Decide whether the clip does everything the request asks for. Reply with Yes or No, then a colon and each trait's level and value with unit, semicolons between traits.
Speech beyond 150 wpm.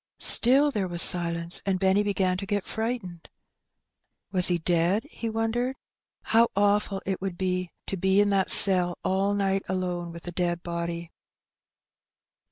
Yes: average, 160 wpm